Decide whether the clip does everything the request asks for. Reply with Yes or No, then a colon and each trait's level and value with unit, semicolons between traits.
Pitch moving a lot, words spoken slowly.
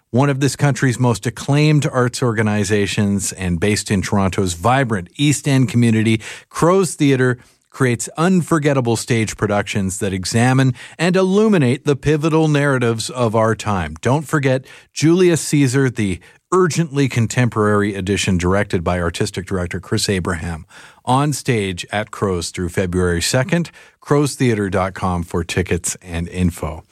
Yes: wide, 6.3 semitones; slow, 130 wpm